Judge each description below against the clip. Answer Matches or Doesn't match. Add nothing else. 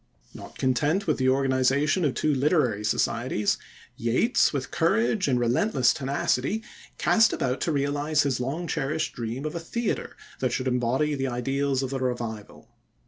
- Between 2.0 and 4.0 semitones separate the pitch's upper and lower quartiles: Matches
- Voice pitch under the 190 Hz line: Matches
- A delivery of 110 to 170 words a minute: Matches